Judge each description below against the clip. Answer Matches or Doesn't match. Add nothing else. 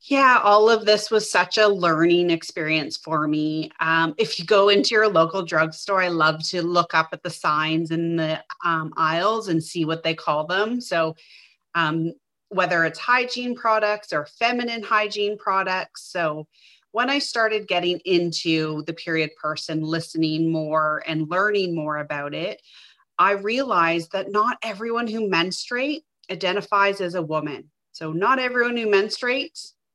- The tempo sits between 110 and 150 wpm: Doesn't match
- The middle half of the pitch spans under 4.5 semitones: Doesn't match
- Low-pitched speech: Doesn't match